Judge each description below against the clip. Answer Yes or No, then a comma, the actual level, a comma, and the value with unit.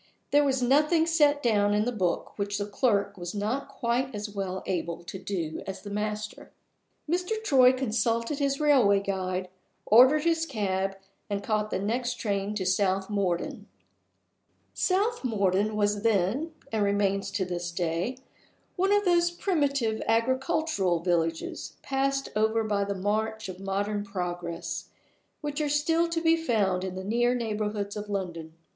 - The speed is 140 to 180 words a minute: Yes, average, 155 wpm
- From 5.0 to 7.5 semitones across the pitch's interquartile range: Yes, wide, 5.6 semitones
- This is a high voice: Yes, high, 210 Hz